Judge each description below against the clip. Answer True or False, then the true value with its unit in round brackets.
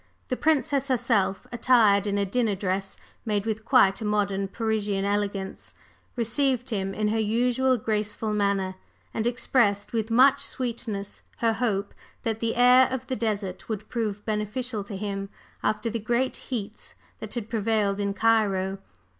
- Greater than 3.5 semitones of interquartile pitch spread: False (3.0 semitones)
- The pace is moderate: True (155 wpm)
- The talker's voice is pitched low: False (215 Hz)